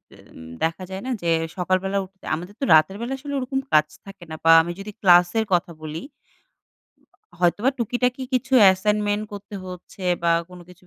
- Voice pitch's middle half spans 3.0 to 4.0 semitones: Yes, average, 3.5 semitones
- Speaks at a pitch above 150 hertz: Yes, high, 190 Hz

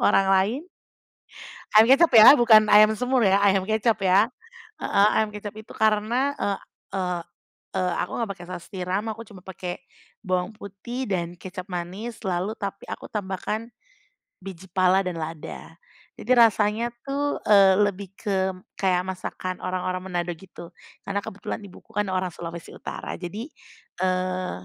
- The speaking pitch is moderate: No, high, 195 Hz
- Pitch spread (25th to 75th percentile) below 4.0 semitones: Yes, average, 2.9 semitones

